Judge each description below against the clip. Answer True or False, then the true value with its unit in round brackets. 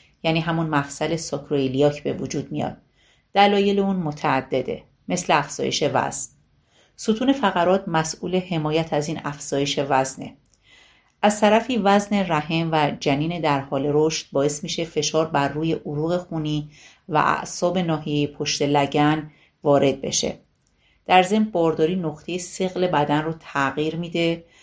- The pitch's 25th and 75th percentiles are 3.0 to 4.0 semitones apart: True (3.3 semitones)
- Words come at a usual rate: True (130 wpm)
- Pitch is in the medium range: True (160 Hz)